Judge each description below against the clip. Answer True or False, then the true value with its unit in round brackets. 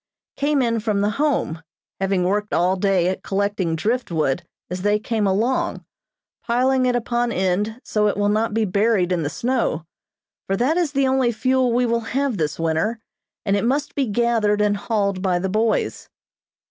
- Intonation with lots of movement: False (4.0 semitones)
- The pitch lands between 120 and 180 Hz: False (210 Hz)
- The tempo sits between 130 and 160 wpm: False (180 wpm)